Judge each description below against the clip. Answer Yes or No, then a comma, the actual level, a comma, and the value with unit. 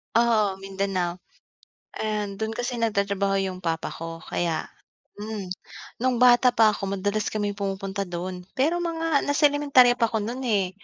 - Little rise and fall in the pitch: No, average, 4.0 semitones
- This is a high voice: Yes, high, 205 Hz